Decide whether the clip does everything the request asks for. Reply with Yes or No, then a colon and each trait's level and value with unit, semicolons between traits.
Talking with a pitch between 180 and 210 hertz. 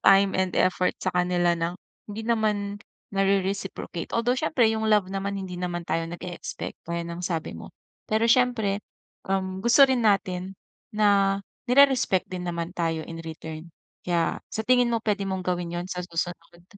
Yes: high, 190 Hz